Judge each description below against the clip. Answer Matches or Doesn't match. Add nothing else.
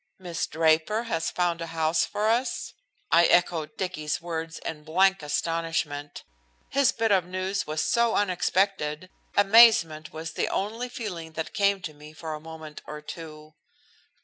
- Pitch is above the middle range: Doesn't match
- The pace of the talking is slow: Doesn't match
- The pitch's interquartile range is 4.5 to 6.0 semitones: Doesn't match